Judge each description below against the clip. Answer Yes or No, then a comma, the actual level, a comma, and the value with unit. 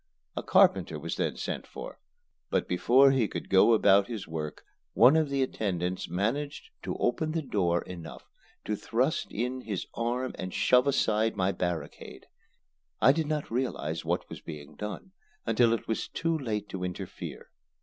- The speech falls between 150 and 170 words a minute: Yes, average, 165 wpm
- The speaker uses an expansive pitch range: Yes, wide, 5.9 semitones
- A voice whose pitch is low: Yes, low, 115 Hz